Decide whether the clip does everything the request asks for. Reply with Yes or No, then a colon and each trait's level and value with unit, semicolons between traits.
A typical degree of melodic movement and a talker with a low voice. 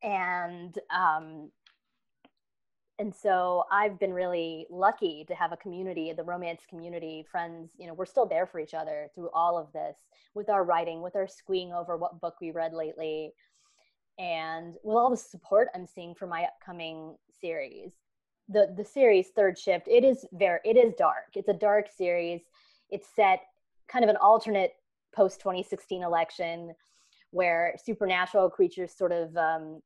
No: average, 3.1 semitones; medium, 180 Hz